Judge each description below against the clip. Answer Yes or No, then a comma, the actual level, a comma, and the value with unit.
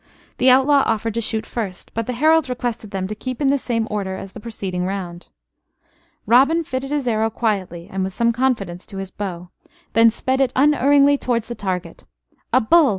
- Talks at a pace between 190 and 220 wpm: Yes, average, 200 wpm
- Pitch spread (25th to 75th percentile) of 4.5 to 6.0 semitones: Yes, average, 5.2 semitones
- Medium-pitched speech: No, high, 230 Hz